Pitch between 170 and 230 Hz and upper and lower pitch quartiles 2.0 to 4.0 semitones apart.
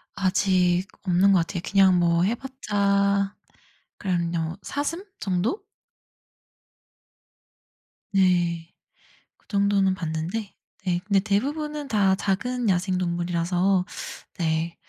Yes: high, 190 Hz; narrow, 2.6 semitones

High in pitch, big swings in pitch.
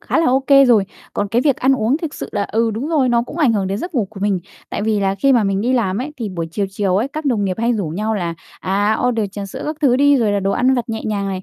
No: high, 220 Hz; average, 4.7 semitones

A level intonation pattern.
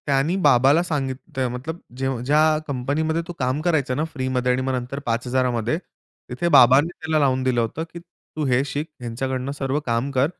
No: average, 3.0 semitones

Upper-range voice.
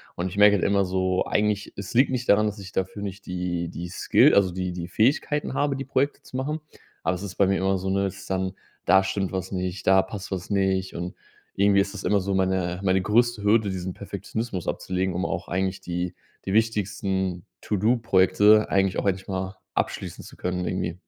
No: very low, 95 Hz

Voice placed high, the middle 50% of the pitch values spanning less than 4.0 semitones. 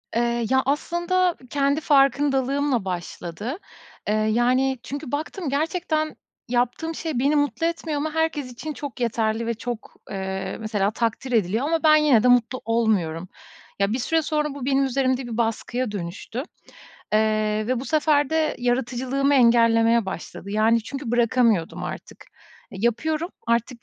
No: very high, 250 Hz; average, 4.3 semitones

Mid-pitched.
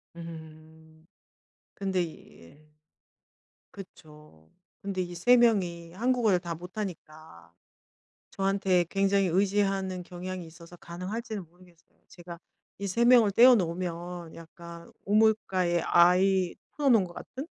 Yes: medium, 180 Hz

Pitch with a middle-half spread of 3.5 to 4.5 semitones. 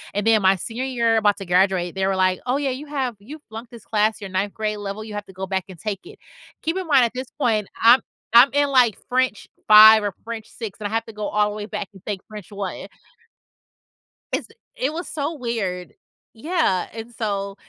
Yes: average, 3.9 semitones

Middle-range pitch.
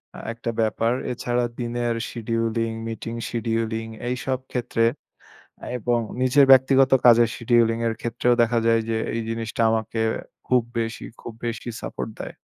No: low, 115 Hz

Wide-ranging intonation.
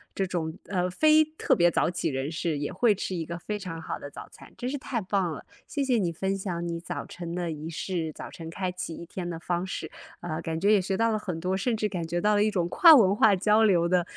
No: average, 3.6 semitones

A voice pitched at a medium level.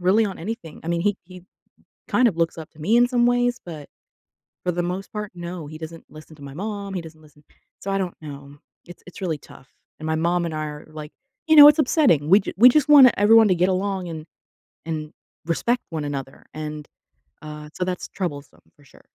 Yes: medium, 175 Hz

